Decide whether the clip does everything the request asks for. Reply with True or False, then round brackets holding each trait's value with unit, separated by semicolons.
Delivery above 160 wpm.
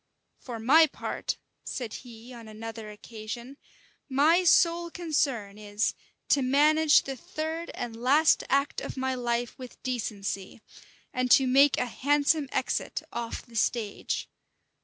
False (135 wpm)